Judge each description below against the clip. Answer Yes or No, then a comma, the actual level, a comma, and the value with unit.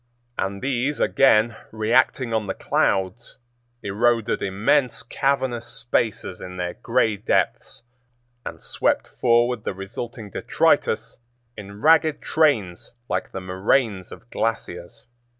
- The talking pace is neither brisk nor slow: No, slow, 115 wpm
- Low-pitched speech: Yes, low, 115 Hz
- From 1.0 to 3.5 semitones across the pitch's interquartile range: No, average, 3.9 semitones